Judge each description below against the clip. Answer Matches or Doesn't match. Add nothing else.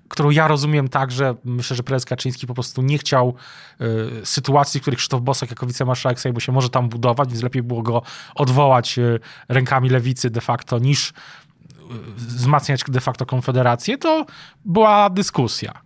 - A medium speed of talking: Doesn't match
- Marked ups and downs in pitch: Doesn't match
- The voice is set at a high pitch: Doesn't match